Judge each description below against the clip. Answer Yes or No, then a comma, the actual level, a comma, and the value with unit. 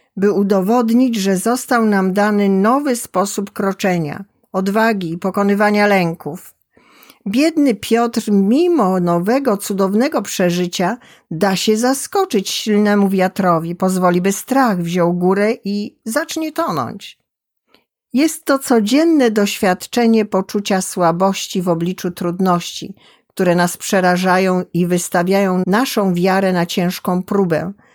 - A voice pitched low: No, high, 200 Hz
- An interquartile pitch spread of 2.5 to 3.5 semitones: No, average, 4.0 semitones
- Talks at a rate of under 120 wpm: Yes, slow, 110 wpm